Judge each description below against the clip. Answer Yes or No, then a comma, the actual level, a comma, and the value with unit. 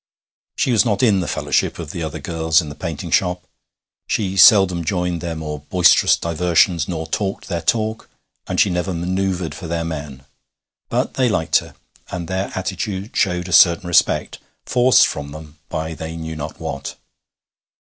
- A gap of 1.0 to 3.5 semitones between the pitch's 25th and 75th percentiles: Yes, average, 2.9 semitones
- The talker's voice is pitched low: Yes, very low, 85 Hz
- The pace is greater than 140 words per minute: Yes, average, 170 wpm